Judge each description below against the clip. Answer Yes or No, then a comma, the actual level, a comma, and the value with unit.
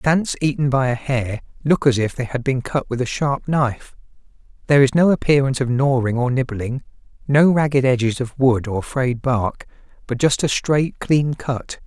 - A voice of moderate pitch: No, low, 130 Hz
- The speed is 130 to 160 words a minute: No, average, 190 wpm